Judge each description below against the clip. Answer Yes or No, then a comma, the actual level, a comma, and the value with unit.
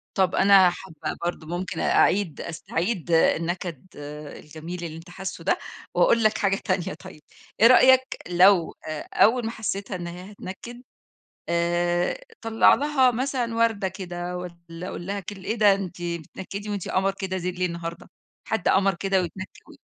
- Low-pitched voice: No, medium, 185 Hz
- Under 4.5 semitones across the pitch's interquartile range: Yes, average, 2.9 semitones